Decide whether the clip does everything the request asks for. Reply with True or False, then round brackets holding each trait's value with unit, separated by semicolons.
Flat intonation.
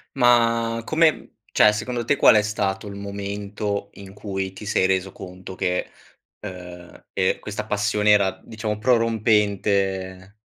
True (2.2 semitones)